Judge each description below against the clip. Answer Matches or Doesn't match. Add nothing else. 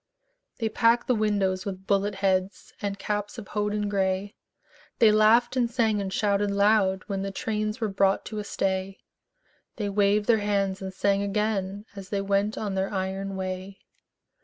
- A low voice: Doesn't match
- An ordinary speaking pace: Matches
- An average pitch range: Doesn't match